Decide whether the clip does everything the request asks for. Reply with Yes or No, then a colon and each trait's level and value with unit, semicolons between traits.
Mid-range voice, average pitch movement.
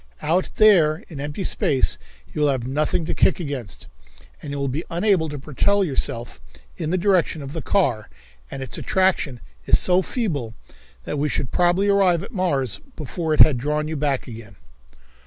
Yes: medium, 150 Hz; average, 5.0 semitones